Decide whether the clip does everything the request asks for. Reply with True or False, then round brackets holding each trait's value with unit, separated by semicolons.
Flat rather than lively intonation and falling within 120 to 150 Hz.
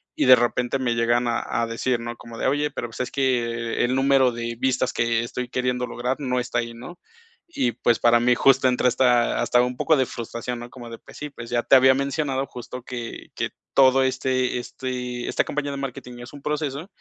True (1.9 semitones; 125 Hz)